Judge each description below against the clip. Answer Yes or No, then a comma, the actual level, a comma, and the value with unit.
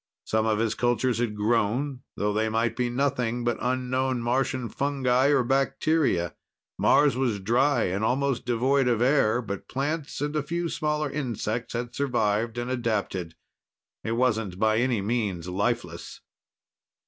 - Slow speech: No, average, 150 wpm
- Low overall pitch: Yes, low, 120 Hz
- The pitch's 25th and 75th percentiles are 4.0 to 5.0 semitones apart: No, average, 3.5 semitones